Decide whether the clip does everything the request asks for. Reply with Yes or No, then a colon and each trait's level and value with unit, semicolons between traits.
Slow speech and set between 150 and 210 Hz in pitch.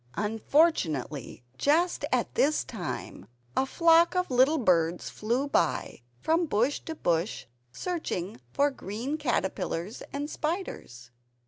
No: slow, 115 wpm; very high, 255 Hz